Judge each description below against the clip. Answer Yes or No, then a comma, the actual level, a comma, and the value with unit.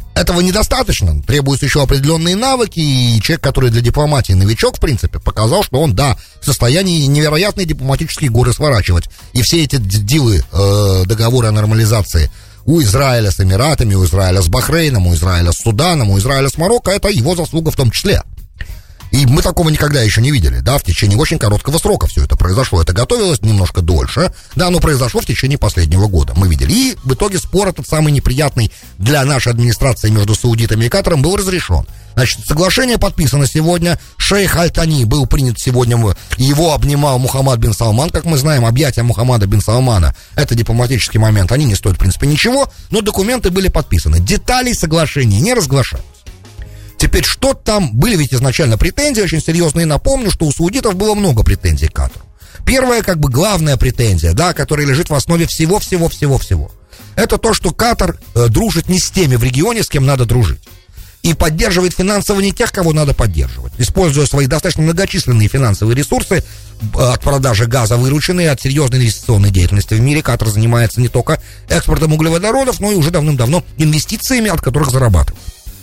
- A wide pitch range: Yes, wide, 7.7 semitones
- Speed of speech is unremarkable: Yes, average, 170 wpm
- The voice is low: Yes, low, 130 Hz